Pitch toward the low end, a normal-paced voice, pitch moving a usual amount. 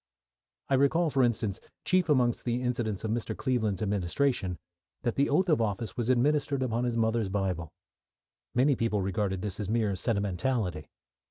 Yes: low, 115 Hz; average, 160 wpm; average, 4.4 semitones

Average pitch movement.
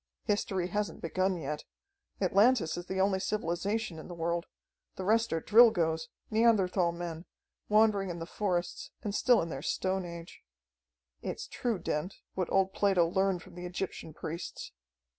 Yes: average, 3.1 semitones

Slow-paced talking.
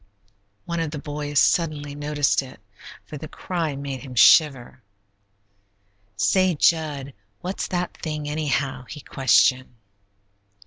Yes: slow, 120 wpm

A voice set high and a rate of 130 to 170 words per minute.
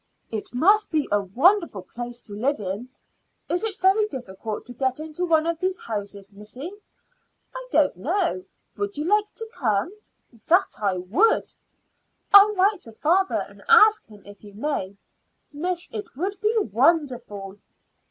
Yes: very high, 295 Hz; average, 155 wpm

